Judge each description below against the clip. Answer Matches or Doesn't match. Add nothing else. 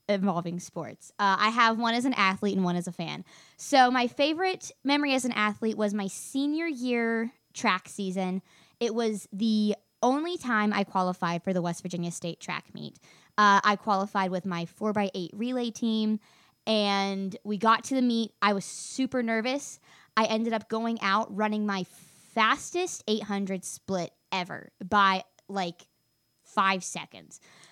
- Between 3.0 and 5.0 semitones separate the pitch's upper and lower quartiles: Matches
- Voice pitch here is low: Doesn't match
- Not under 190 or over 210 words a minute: Doesn't match